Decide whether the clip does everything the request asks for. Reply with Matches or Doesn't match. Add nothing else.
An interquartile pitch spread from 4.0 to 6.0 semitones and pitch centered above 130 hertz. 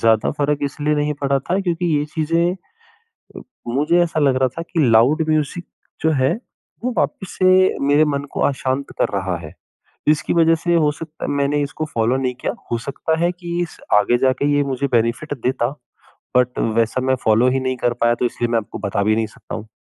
Matches